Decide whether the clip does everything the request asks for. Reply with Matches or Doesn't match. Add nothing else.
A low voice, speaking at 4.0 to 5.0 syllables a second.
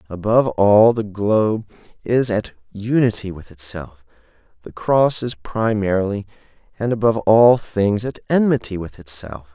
Matches